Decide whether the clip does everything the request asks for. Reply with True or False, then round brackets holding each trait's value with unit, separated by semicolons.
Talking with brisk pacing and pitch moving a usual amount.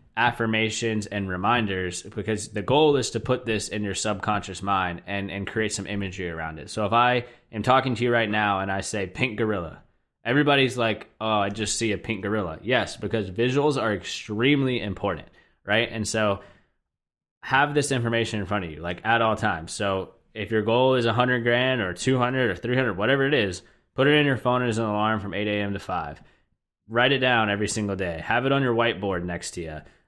True (215 wpm; 3.4 semitones)